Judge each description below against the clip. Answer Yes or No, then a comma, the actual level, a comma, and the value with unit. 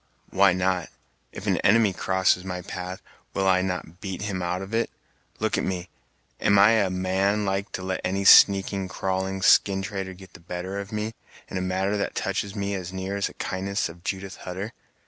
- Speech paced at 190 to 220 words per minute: Yes, average, 200 wpm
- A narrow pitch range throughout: Yes, narrow, 1.2 semitones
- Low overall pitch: Yes, very low, 95 Hz